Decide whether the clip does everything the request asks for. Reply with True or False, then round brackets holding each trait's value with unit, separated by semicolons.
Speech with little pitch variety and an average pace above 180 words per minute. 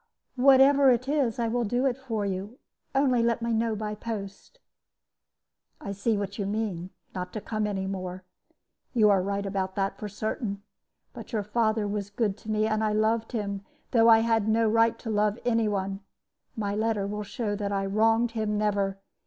True (2.2 semitones; 190 wpm)